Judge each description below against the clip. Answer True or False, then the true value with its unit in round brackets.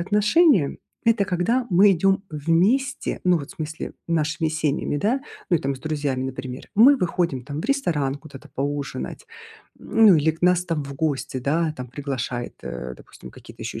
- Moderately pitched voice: True (160 Hz)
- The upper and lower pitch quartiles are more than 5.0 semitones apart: True (5.5 semitones)